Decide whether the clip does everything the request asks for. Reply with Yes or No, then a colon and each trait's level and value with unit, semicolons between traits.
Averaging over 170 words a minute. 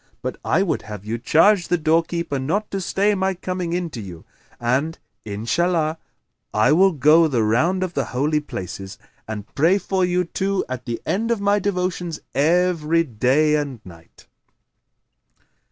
No: average, 160 wpm